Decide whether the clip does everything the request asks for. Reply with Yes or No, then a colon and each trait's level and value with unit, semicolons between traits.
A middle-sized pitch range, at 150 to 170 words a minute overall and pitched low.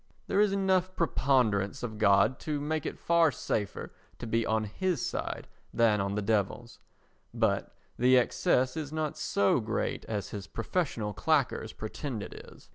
No: wide, 6.6 semitones; average, 160 wpm; low, 120 Hz